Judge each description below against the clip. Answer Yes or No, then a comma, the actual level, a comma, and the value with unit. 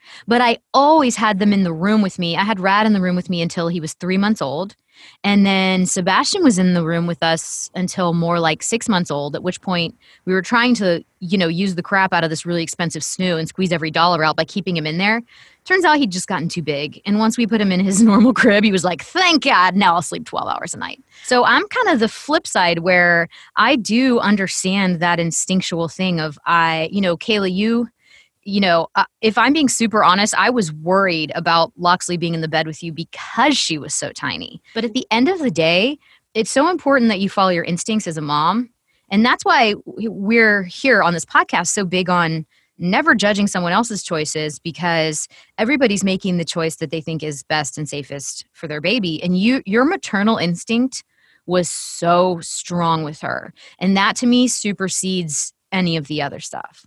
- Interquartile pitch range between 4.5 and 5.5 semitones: Yes, average, 5.0 semitones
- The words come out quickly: Yes, fast, 220 wpm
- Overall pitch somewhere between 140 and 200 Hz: Yes, medium, 185 Hz